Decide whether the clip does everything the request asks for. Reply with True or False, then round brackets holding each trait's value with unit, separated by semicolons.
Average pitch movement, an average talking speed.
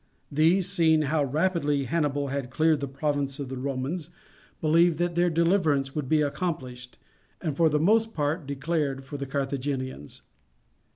True (3.2 semitones; 155 wpm)